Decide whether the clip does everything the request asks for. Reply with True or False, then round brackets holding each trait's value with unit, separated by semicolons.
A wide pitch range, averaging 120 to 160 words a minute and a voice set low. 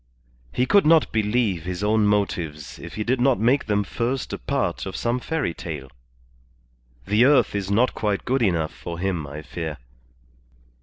False (6.2 semitones; 170 wpm; 105 Hz)